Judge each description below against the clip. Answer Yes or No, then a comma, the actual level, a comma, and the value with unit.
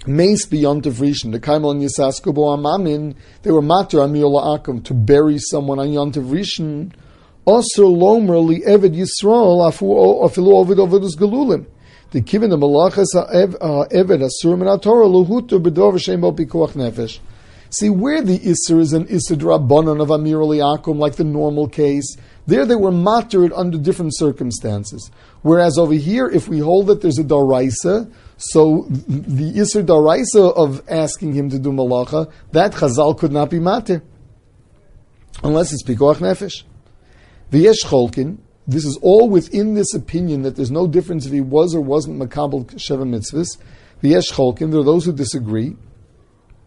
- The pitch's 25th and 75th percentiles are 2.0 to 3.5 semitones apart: No, average, 4.5 semitones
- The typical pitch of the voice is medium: Yes, medium, 155 Hz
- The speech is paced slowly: Yes, slow, 130 wpm